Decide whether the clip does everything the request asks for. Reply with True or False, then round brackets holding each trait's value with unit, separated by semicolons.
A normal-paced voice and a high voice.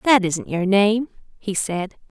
True (165 wpm; 200 Hz)